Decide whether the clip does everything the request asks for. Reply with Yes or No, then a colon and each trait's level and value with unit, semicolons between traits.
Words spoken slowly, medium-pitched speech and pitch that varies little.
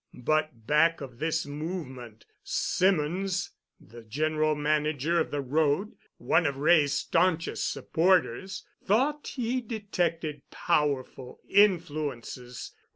No: slow, 100 wpm; medium, 155 Hz; average, 4.1 semitones